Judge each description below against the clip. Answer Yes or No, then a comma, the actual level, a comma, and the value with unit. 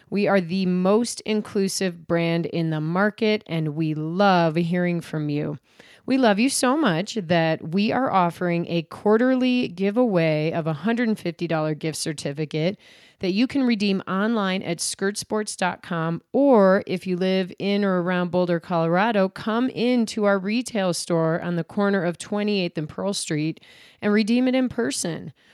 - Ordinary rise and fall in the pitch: Yes, average, 4.2 semitones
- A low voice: No, high, 190 Hz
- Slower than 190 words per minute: Yes, average, 155 wpm